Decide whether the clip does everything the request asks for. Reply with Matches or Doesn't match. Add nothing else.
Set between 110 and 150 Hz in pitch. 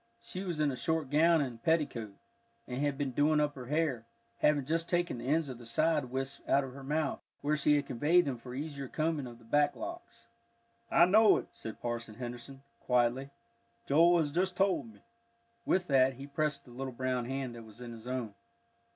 Matches